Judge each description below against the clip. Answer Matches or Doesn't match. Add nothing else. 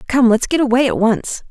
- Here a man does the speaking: Doesn't match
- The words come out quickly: Matches